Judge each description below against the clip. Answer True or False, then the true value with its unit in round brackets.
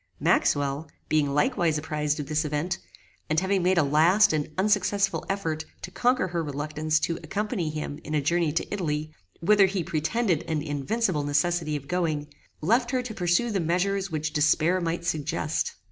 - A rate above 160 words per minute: True (170 wpm)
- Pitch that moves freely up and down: False (3.8 semitones)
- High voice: False (165 Hz)